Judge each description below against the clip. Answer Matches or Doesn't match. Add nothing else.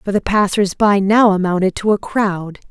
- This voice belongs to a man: Doesn't match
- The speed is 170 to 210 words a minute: Matches